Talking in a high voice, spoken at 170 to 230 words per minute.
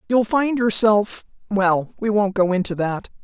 No: high, 205 Hz; average, 150 wpm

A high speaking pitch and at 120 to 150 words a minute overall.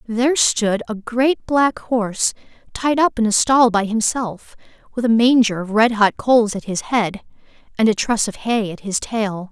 No: high, 225 Hz; average, 195 wpm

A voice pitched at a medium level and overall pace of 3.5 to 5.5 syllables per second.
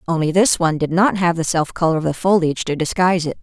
No: medium, 170 Hz; 6.8 syllables/s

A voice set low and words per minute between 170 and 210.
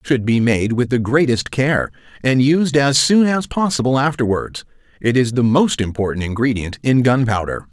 Yes: low, 130 Hz; average, 180 wpm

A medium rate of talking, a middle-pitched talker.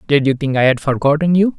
No: fast, 265 wpm; medium, 145 Hz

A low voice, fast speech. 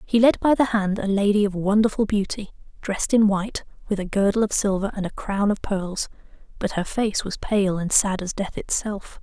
No: high, 205 Hz; fast, 215 wpm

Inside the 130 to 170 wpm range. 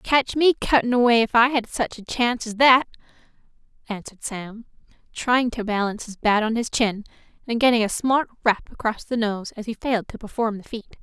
No: average, 200 wpm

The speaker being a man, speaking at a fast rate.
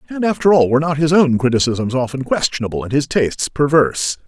No: male; average, 195 wpm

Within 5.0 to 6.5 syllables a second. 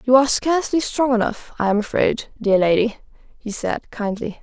Yes: 5.1 syllables/s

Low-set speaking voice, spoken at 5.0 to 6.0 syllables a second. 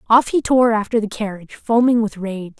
No: high, 220 Hz; 5.4 syllables/s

